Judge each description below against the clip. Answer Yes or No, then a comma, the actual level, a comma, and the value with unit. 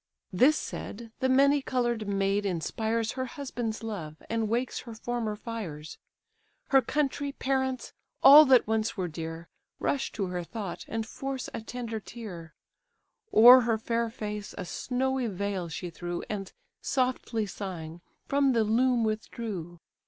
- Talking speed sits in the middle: Yes, average, 145 wpm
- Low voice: No, high, 225 Hz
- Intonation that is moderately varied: Yes, average, 4.4 semitones